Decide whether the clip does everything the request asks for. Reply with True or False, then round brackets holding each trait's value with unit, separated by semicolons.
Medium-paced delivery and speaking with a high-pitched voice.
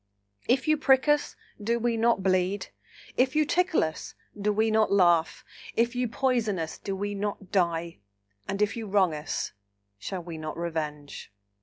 True (170 wpm; 205 Hz)